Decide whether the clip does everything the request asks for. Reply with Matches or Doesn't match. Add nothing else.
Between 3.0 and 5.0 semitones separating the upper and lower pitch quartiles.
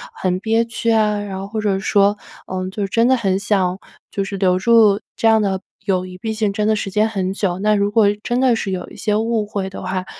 Doesn't match